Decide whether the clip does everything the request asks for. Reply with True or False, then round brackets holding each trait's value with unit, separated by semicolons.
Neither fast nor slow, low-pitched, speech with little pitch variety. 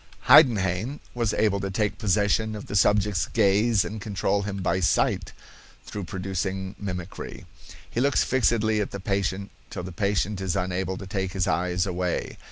True (165 wpm; 100 Hz; 2.2 semitones)